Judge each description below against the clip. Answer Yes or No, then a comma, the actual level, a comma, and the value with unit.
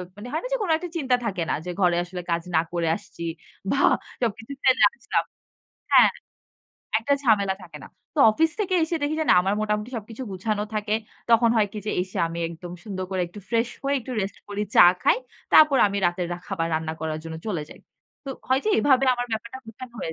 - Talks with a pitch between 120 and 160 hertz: No, high, 210 Hz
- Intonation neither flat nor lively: No, wide, 6.1 semitones